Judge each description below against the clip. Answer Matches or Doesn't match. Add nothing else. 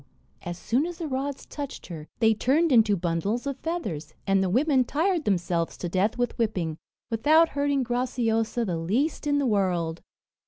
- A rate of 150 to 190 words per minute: Matches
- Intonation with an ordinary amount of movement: Doesn't match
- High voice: Matches